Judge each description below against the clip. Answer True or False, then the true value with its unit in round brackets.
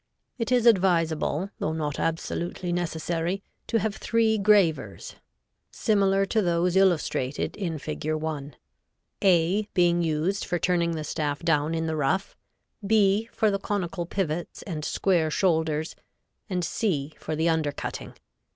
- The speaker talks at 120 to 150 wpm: True (140 wpm)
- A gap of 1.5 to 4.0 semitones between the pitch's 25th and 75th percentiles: True (3.7 semitones)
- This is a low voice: False (175 Hz)